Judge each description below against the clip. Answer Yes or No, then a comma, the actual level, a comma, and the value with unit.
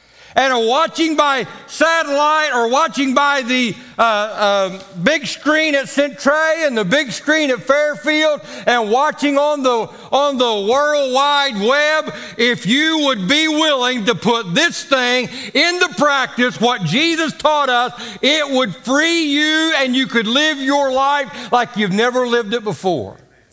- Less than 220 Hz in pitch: No, very high, 275 Hz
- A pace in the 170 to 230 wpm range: No, average, 155 wpm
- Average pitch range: Yes, average, 3.8 semitones